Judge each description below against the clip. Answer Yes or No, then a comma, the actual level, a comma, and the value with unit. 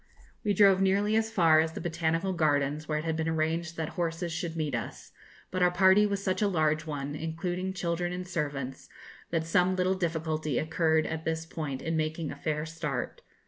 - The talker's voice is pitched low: No, medium, 165 Hz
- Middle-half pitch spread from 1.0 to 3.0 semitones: Yes, narrow, 2.5 semitones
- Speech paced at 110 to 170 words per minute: No, average, 195 wpm